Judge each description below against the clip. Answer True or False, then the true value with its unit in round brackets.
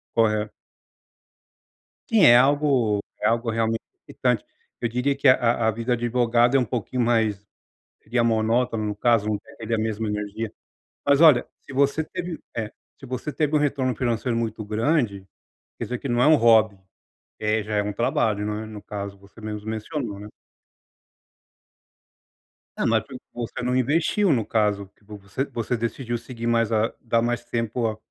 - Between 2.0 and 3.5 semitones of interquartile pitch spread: True (2.8 semitones)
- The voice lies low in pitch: True (115 Hz)